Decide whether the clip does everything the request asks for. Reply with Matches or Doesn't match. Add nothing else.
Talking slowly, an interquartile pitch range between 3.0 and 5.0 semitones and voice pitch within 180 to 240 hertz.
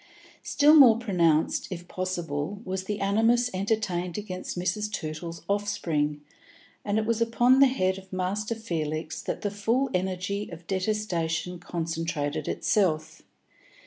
Matches